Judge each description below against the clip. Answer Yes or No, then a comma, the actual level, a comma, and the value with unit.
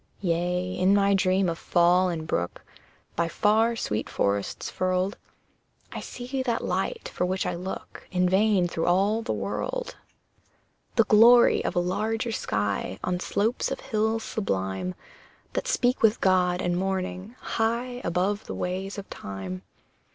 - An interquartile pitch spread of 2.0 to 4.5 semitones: Yes, average, 3.8 semitones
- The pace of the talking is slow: No, average, 150 wpm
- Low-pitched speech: No, medium, 185 Hz